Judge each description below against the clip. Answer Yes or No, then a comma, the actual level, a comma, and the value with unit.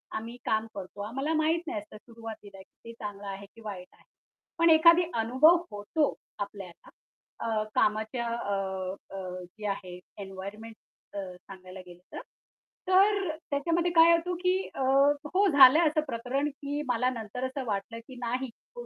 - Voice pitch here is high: Yes, high, 230 Hz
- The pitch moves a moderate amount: No, wide, 7.3 semitones